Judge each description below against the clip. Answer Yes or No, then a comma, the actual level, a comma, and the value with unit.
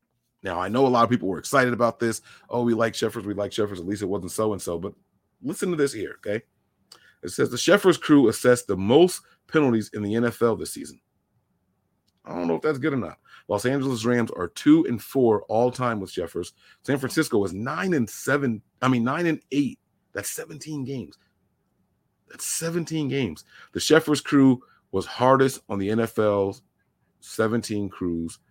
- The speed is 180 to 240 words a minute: Yes, average, 190 wpm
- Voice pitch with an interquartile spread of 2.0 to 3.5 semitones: No, average, 5.1 semitones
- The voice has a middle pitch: No, low, 120 Hz